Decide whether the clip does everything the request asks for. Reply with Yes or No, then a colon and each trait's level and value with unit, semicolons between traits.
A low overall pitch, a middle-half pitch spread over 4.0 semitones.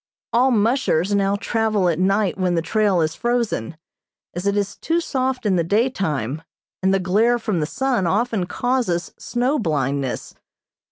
No: high, 200 Hz; wide, 5.5 semitones